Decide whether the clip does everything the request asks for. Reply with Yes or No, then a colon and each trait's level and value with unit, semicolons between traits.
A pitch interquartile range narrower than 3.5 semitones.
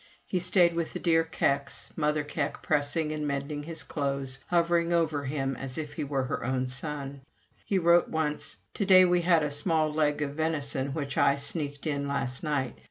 Yes: narrow, 2.6 semitones